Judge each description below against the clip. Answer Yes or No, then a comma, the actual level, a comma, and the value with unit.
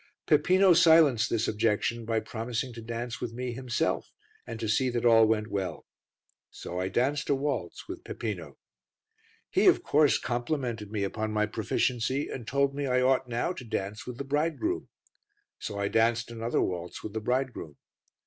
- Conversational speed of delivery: Yes, average, 170 wpm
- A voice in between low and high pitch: No, low, 120 Hz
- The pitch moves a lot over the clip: No, average, 3.5 semitones